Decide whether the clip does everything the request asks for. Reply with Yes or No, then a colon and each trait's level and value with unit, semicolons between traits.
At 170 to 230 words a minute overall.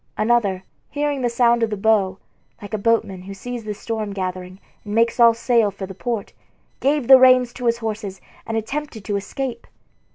Yes: average, 190 wpm